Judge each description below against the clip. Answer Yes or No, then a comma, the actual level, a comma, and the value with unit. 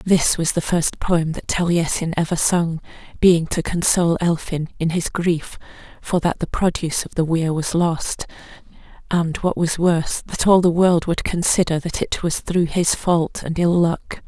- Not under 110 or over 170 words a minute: No, average, 185 wpm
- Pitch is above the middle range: No, medium, 170 Hz